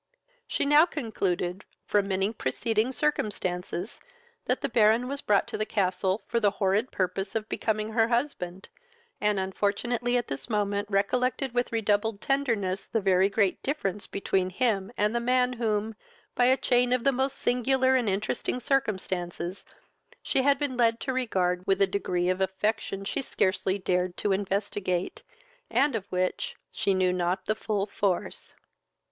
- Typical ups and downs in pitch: Yes, average, 4.3 semitones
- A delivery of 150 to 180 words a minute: Yes, average, 160 wpm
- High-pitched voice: Yes, high, 210 Hz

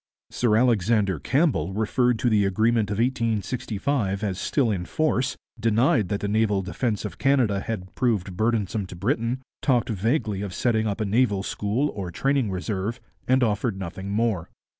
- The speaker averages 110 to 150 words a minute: No, average, 165 wpm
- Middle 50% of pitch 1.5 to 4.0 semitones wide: Yes, average, 3.7 semitones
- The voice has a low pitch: Yes, low, 110 Hz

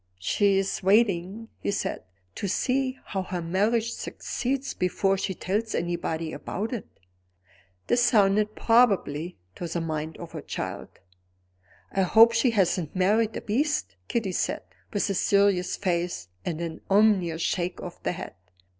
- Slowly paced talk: No, average, 145 wpm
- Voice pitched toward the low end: No, high, 195 Hz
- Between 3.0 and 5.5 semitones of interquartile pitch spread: Yes, average, 4.2 semitones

